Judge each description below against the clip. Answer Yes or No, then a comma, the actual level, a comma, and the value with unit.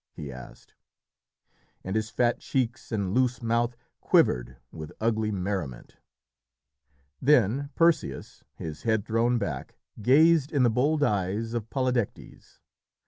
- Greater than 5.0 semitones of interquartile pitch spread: No, average, 4.7 semitones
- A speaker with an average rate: No, slow, 120 wpm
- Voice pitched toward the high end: No, low, 115 Hz